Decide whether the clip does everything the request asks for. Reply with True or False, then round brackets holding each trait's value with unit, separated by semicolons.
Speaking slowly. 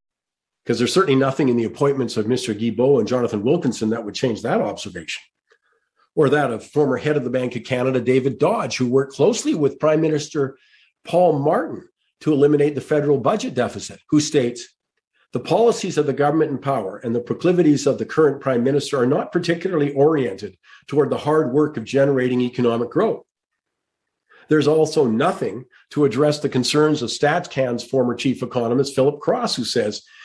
False (175 wpm)